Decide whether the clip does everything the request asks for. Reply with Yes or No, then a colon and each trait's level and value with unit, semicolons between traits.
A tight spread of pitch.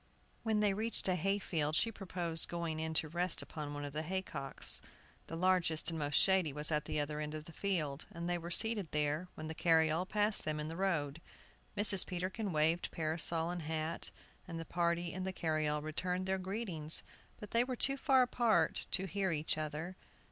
No: average, 3.5 semitones